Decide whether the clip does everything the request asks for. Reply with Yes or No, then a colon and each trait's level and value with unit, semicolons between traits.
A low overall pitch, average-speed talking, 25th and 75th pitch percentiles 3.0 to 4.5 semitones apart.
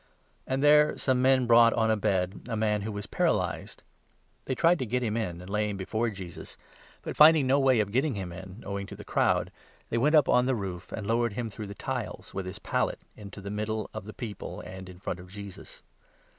No: low, 110 Hz; fast, 235 wpm; average, 4.0 semitones